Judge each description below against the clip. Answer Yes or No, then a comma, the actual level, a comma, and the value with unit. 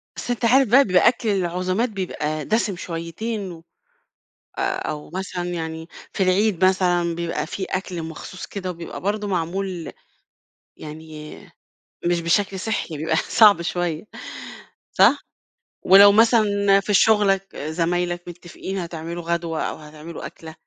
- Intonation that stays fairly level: No, average, 3.1 semitones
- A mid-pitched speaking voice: Yes, medium, 180 Hz